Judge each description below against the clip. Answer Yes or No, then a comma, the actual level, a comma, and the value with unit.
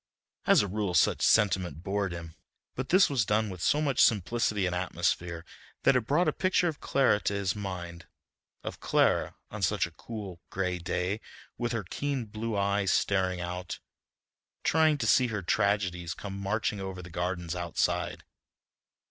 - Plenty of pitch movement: No, average, 4.0 semitones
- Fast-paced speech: No, average, 165 wpm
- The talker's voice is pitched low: Yes, low, 100 Hz